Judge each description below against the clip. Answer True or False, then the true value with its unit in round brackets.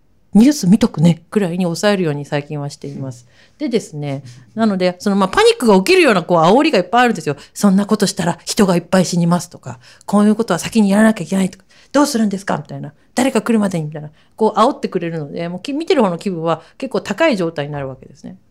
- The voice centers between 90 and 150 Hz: False (185 Hz)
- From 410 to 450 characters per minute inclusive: True (445 characters per minute)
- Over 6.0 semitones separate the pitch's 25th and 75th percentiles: False (5.4 semitones)